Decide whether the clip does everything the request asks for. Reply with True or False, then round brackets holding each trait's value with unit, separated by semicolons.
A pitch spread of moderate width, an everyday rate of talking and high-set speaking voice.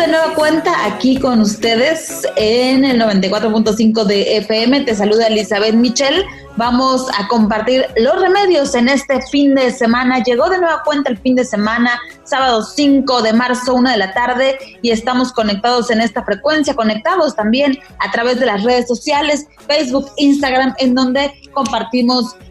True (3.3 semitones; 160 wpm; 250 Hz)